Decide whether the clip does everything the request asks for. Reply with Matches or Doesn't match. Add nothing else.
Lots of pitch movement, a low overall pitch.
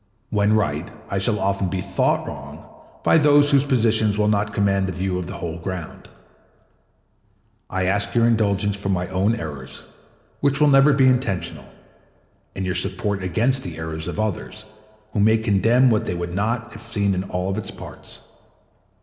Doesn't match